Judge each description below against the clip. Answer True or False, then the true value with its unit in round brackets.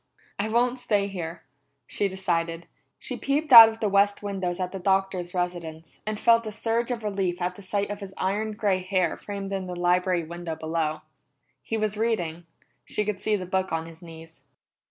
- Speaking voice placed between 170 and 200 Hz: True (190 Hz)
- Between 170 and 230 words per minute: True (195 wpm)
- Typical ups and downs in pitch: True (3.2 semitones)